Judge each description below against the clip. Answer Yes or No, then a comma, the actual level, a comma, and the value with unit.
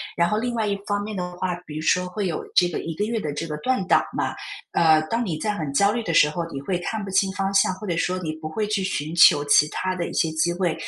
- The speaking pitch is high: No, medium, 180 Hz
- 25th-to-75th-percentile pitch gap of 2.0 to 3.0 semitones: No, average, 4.1 semitones